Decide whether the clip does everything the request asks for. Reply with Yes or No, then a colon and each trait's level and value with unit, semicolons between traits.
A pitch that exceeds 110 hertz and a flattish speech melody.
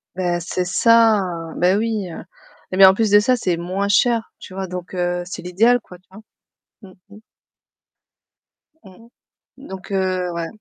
No: high, 190 Hz; average, 3.1 semitones